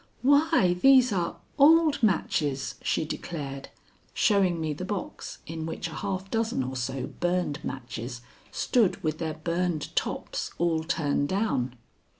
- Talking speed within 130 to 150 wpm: Yes, average, 140 wpm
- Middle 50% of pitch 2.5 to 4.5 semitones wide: No, wide, 5.5 semitones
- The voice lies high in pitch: No, medium, 170 Hz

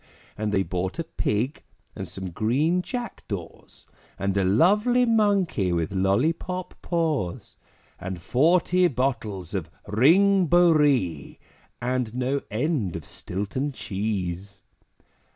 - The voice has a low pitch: Yes, low, 120 Hz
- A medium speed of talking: No, slow, 115 wpm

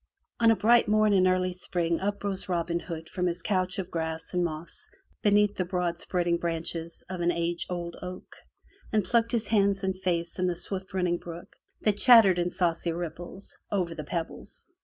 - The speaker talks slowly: No, average, 190 wpm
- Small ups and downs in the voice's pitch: Yes, narrow, 2.3 semitones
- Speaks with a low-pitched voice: No, medium, 180 Hz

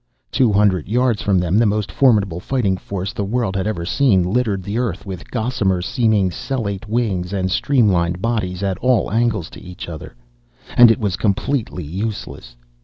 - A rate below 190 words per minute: Yes, average, 175 wpm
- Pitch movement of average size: Yes, average, 4.1 semitones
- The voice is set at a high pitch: No, low, 100 Hz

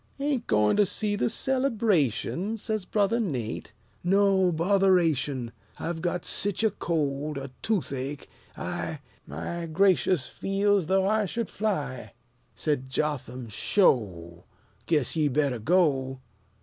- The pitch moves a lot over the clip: Yes, wide, 6.9 semitones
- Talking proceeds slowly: Yes, slow, 120 wpm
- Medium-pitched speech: Yes, medium, 170 Hz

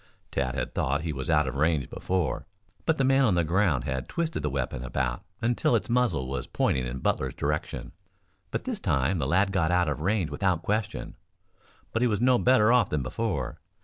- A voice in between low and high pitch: No, very low, 85 Hz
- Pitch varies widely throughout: Yes, wide, 8.3 semitones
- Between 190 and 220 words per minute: Yes, fast, 205 wpm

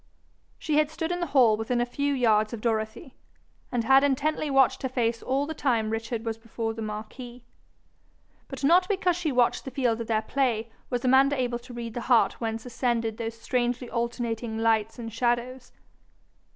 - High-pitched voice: Yes, high, 240 Hz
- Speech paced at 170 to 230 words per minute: Yes, average, 185 wpm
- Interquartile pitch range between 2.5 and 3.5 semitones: Yes, average, 2.8 semitones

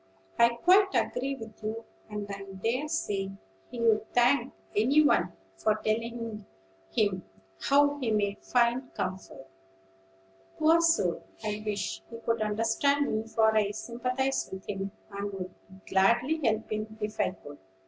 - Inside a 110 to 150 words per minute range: Yes, average, 140 wpm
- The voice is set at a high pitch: Yes, high, 220 Hz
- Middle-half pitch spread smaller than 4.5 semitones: Yes, average, 3.6 semitones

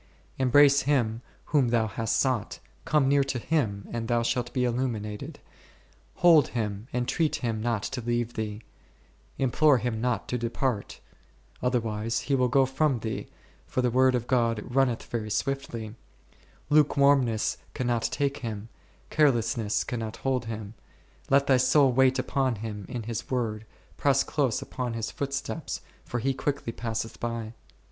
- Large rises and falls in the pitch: No, average, 3.0 semitones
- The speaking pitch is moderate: No, low, 120 Hz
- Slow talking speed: No, average, 155 wpm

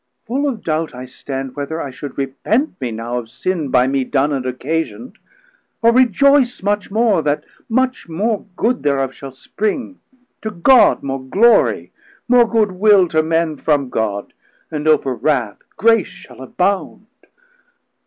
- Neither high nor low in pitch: Yes, medium, 160 Hz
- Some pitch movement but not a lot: No, wide, 8.4 semitones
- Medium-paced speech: Yes, average, 155 wpm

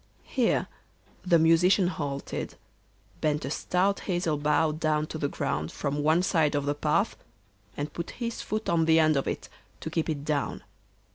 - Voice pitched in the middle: Yes, medium, 155 Hz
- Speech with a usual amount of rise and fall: Yes, average, 3.0 semitones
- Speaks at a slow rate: No, average, 170 wpm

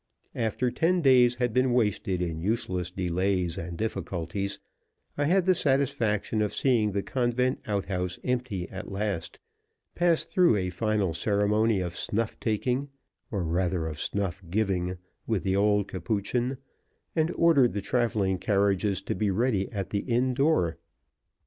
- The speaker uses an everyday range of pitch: Yes, average, 4.8 semitones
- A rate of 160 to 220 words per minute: No, average, 145 wpm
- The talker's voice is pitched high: No, low, 105 Hz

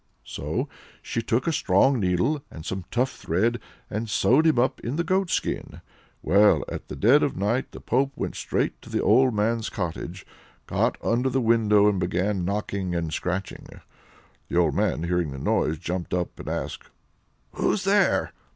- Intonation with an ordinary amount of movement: No, wide, 6.1 semitones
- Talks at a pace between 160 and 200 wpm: Yes, average, 170 wpm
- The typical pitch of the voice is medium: No, low, 105 Hz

